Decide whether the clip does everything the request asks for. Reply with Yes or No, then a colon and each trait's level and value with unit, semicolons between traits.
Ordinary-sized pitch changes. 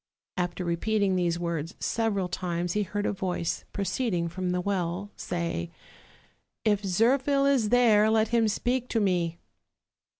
Yes: average, 4.0 semitones